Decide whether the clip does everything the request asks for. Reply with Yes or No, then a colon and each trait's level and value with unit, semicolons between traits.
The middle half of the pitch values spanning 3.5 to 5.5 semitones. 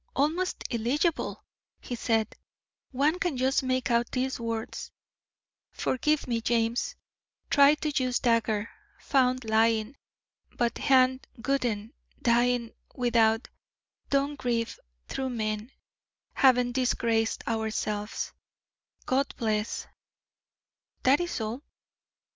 No: average, 2.9 semitones